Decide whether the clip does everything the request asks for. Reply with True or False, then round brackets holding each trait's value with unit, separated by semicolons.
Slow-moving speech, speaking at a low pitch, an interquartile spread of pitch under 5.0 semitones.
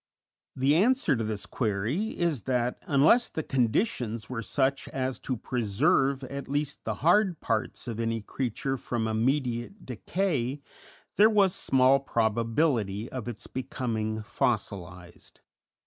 True (130 wpm; 130 Hz; 4.1 semitones)